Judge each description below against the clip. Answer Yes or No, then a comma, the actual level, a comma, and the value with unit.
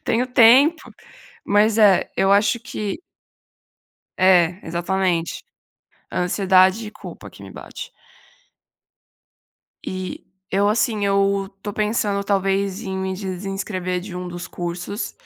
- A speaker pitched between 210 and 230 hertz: No, high, 195 Hz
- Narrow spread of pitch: Yes, narrow, 2.1 semitones